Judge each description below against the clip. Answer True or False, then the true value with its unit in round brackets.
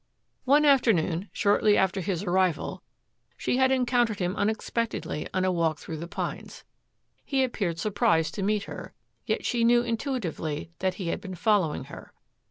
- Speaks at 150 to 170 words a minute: True (160 wpm)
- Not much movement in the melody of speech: False (5.2 semitones)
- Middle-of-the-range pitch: False (200 Hz)